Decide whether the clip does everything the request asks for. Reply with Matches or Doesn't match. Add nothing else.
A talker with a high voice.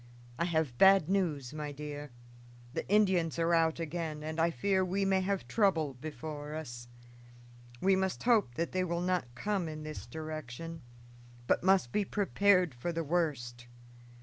Doesn't match